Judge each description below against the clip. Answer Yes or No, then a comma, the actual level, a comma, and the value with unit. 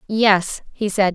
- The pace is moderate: Yes, average, 155 wpm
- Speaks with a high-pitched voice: Yes, high, 200 Hz